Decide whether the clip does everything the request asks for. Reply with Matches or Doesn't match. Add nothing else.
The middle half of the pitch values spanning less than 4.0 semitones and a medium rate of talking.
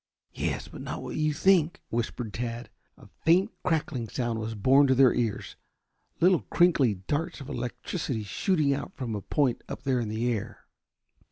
Doesn't match